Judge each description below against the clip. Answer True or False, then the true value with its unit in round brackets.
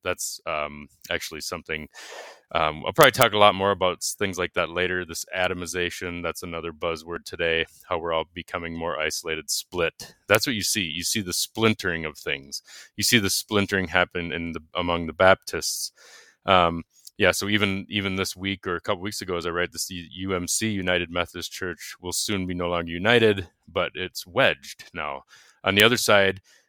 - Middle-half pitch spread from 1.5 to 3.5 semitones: True (2.6 semitones)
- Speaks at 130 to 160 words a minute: False (185 wpm)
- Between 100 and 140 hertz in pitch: False (90 Hz)